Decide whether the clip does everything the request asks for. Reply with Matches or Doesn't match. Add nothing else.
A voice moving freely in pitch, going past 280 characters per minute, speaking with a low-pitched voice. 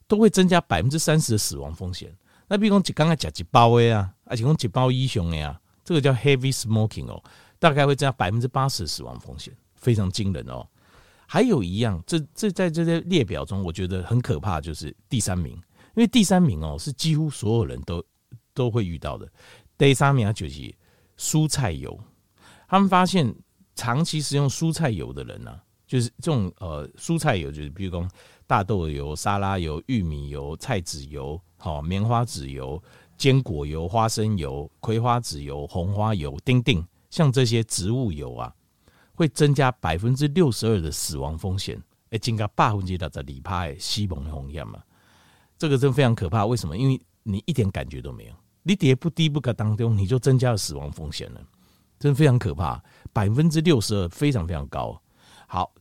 Matches